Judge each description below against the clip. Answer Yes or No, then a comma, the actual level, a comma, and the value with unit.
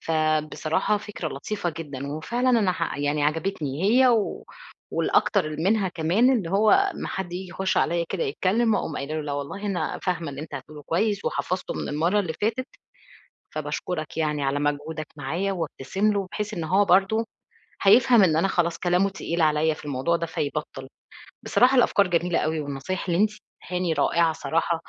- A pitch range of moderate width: Yes, average, 4.5 semitones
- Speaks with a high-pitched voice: No, medium, 170 Hz